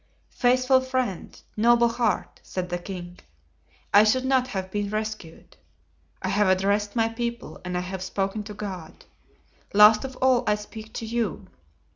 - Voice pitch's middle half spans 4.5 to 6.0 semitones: No, average, 3.8 semitones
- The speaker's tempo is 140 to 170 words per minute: Yes, average, 155 wpm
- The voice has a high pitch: Yes, high, 210 Hz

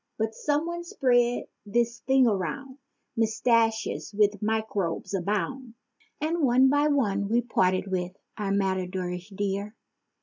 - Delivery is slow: Yes, slow, 115 wpm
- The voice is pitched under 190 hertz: No, high, 220 Hz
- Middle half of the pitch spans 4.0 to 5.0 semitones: Yes, average, 4.6 semitones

